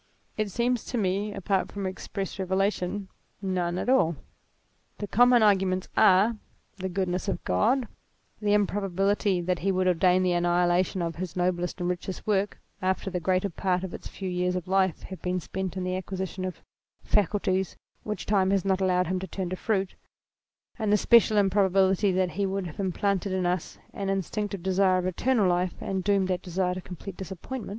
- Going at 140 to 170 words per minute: No, average, 185 wpm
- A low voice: No, high, 190 Hz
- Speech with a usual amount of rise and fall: No, narrow, 1.6 semitones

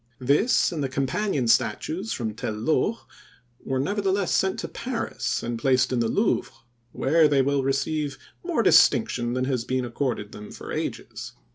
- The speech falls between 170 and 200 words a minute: No, average, 160 wpm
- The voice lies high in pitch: No, low, 135 Hz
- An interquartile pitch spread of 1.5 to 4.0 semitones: No, average, 5.3 semitones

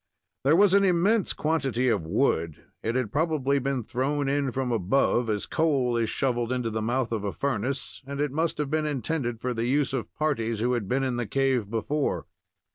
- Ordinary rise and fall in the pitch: Yes, average, 3.8 semitones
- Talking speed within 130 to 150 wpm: No, average, 200 wpm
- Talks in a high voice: No, low, 130 Hz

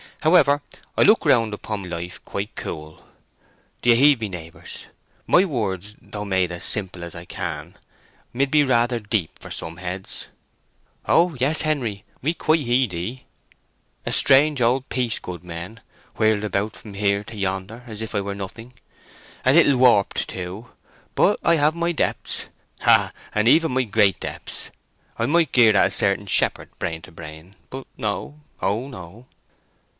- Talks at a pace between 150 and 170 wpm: Yes, average, 160 wpm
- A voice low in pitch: Yes, low, 110 Hz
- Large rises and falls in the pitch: Yes, wide, 5.7 semitones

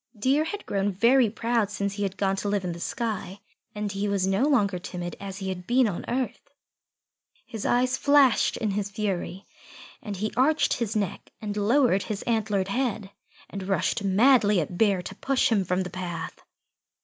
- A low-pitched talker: No, high, 205 Hz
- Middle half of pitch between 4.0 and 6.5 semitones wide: No, average, 3.6 semitones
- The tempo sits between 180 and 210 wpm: Yes, average, 185 wpm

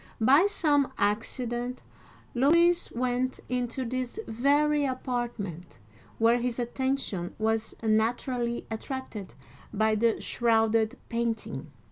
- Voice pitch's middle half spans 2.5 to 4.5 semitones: Yes, average, 2.8 semitones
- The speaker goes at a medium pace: No, slow, 95 wpm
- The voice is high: Yes, high, 240 Hz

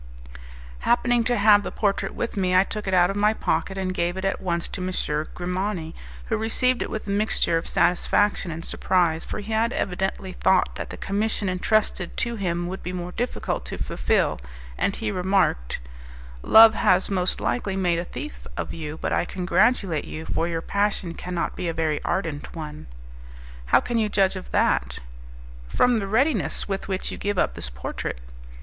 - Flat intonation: No, average, 3.5 semitones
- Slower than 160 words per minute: No, average, 190 wpm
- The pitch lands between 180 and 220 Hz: Yes, high, 190 Hz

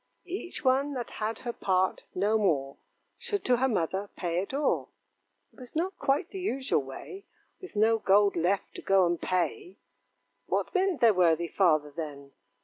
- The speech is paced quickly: No, average, 170 wpm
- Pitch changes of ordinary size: No, wide, 7.9 semitones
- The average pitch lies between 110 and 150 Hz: No, high, 210 Hz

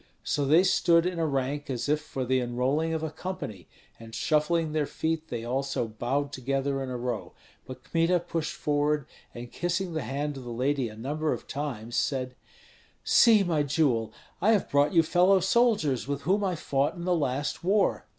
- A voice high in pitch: No, medium, 145 Hz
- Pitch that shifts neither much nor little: Yes, average, 4.3 semitones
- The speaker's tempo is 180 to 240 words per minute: Yes, average, 190 wpm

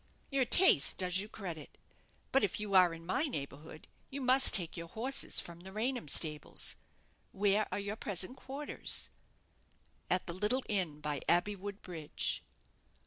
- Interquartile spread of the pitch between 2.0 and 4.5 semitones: No, average, 5.3 semitones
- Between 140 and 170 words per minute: Yes, average, 150 wpm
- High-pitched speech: Yes, high, 195 Hz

